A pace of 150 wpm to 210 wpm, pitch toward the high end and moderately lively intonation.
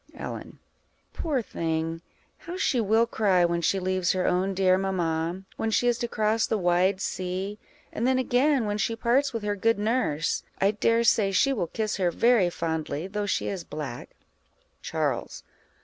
Yes: average, 180 wpm; high, 200 Hz; average, 4.4 semitones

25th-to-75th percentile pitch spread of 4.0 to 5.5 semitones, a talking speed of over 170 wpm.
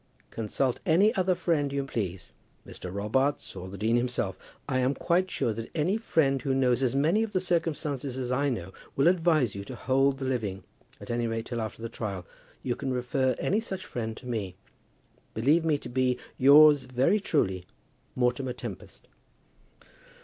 Yes: average, 4.6 semitones; average, 180 wpm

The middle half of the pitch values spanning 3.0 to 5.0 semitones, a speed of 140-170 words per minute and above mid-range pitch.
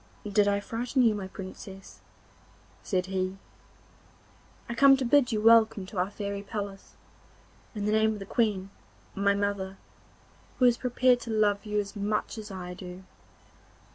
No: narrow, 2.6 semitones; average, 160 wpm; high, 205 Hz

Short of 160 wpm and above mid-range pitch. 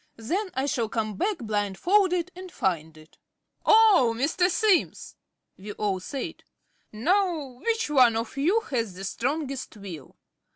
Yes: slow, 135 wpm; very high, 260 Hz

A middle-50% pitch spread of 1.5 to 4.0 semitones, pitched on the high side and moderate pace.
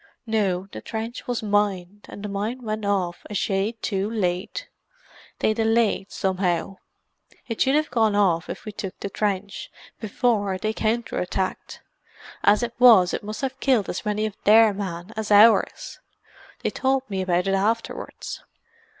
Yes: average, 2.7 semitones; high, 210 Hz; average, 160 wpm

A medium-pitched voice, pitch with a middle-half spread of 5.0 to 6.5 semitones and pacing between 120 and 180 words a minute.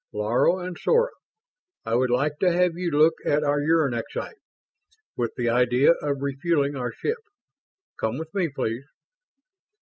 Yes: medium, 145 Hz; wide, 5.4 semitones; average, 145 wpm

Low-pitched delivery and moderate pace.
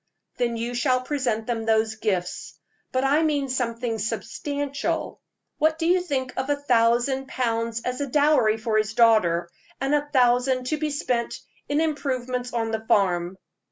No: very high, 250 Hz; average, 160 wpm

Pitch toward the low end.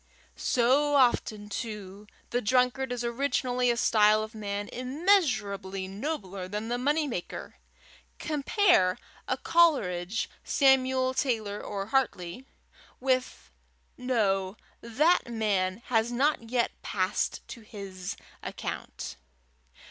No: high, 235 Hz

